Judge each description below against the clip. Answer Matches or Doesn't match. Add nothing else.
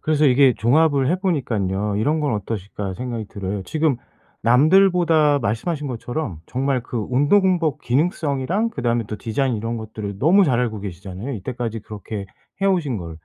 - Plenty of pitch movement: Matches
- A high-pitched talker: Doesn't match